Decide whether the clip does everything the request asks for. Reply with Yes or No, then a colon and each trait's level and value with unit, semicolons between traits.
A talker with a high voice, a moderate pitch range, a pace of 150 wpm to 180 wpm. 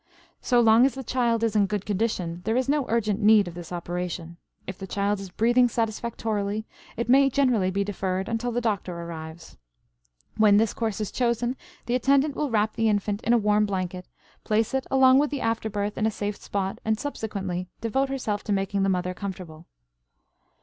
No: high, 215 Hz; average, 3.5 semitones; average, 195 wpm